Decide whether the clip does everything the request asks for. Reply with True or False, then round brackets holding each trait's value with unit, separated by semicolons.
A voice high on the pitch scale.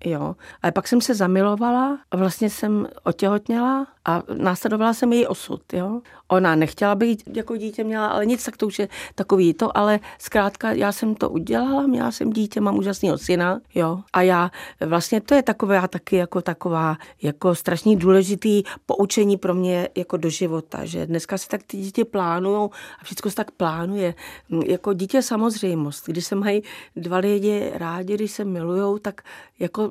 True (200 Hz)